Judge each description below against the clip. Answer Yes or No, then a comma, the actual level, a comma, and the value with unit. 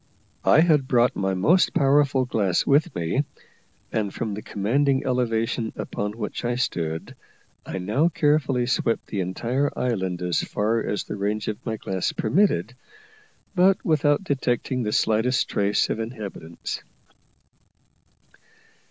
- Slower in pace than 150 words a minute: Yes, slow, 135 wpm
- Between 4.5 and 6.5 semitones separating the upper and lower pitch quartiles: Yes, average, 5.1 semitones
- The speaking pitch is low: Yes, low, 115 Hz